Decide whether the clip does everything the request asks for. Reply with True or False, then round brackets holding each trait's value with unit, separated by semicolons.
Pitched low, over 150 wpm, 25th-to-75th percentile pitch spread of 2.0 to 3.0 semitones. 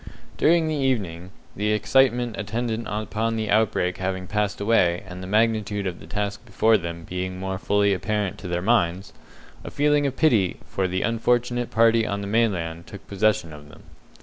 False (105 Hz; 175 wpm; 3.6 semitones)